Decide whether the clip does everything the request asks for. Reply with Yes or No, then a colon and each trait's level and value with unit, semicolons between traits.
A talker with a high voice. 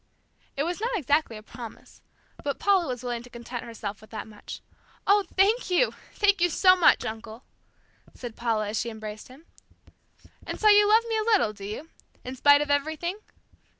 Yes: very high, 285 Hz